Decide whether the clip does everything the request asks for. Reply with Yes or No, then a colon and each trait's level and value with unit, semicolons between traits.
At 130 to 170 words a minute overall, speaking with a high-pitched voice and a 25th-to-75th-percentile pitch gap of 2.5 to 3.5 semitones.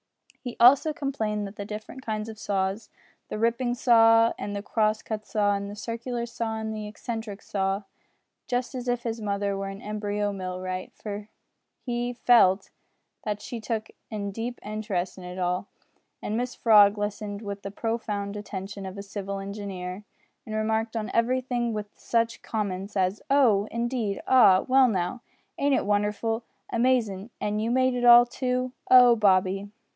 Yes: average, 165 wpm; high, 215 Hz; average, 2.9 semitones